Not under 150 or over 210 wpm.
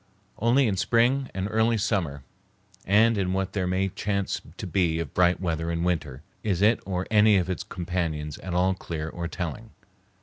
Yes: average, 180 wpm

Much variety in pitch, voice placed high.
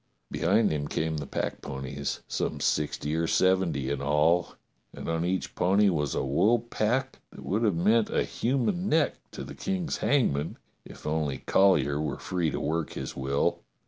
No: wide, 6.8 semitones; very low, 85 Hz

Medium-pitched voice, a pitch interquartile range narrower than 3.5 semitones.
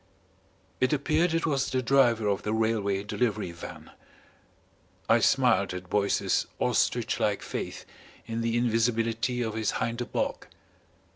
No: low, 115 Hz; average, 3.1 semitones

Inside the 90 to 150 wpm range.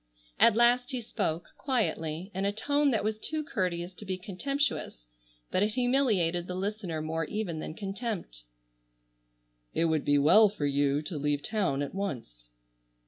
No: average, 160 wpm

